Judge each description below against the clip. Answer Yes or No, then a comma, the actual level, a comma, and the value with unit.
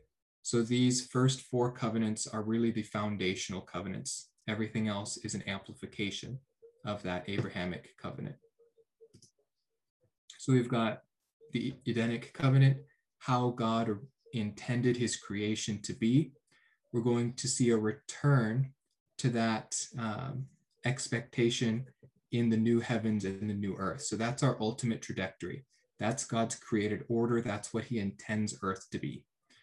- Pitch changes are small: No, average, 3.0 semitones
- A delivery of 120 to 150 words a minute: Yes, slow, 135 wpm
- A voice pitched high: No, low, 115 Hz